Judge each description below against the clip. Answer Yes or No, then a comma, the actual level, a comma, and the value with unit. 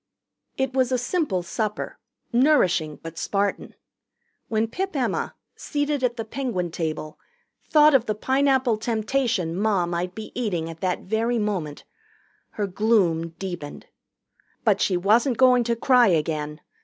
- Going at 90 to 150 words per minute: Yes, average, 140 wpm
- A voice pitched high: Yes, high, 215 Hz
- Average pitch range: No, wide, 6.2 semitones